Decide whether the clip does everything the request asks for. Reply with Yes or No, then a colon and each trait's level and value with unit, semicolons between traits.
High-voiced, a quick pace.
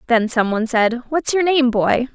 No: very high, 250 Hz; average, 195 wpm